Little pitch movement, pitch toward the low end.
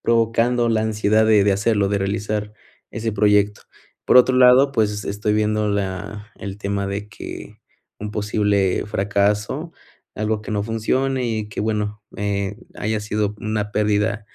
Yes: narrow, 1.3 semitones; low, 105 Hz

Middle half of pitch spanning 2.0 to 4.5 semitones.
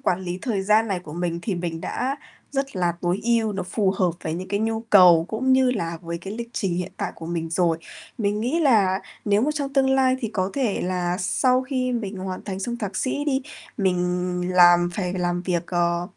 No: average, 5.2 semitones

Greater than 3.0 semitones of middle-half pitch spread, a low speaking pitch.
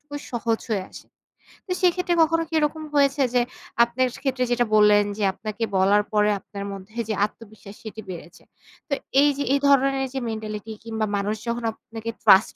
No: average, 4.7 semitones; high, 225 Hz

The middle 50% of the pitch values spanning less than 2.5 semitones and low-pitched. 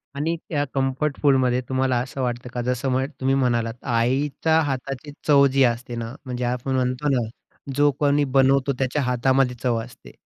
Yes: narrow, 1.9 semitones; low, 130 Hz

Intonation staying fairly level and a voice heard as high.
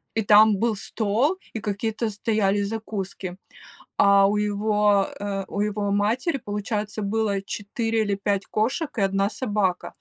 Yes: narrow, 1.7 semitones; high, 210 Hz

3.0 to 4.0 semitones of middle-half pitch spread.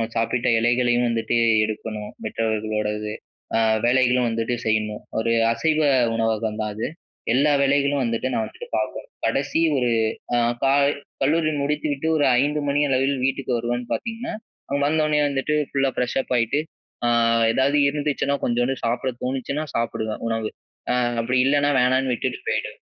Yes: average, 3.7 semitones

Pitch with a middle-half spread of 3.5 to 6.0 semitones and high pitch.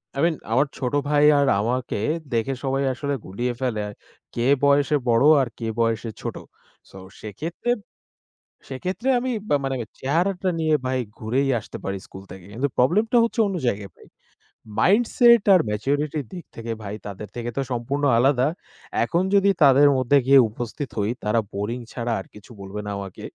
No: average, 4.6 semitones; low, 130 Hz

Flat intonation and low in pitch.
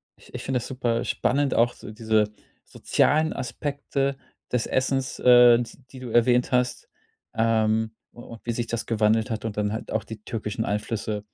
Yes: narrow, 2.3 semitones; low, 115 Hz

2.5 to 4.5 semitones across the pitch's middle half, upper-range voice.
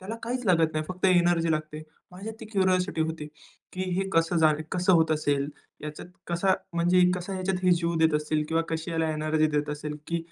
No: average, 2.9 semitones; medium, 165 Hz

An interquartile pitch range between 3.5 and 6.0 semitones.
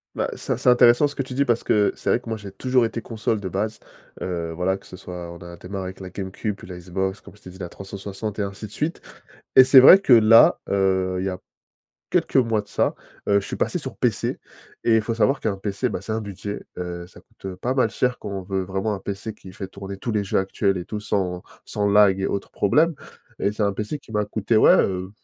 No: average, 2.8 semitones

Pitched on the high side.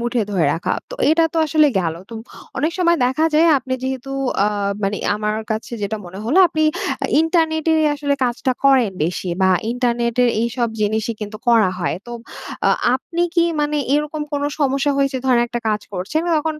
Yes: very high, 260 Hz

